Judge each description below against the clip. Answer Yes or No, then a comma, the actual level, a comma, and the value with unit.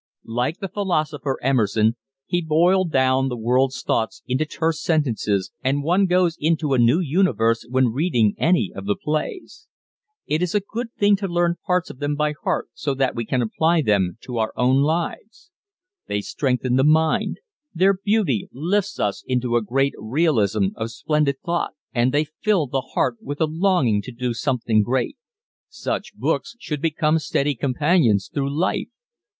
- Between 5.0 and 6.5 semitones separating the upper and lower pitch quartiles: Yes, wide, 5.6 semitones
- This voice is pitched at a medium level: Yes, medium, 145 Hz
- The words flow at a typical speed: Yes, average, 170 wpm